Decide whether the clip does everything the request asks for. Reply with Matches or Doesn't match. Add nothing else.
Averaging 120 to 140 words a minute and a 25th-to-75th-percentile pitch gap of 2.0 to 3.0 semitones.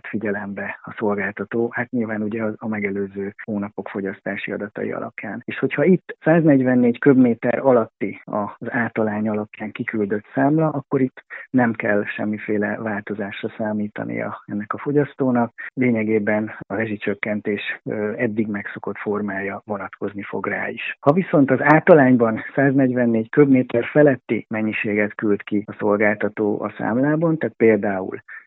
Doesn't match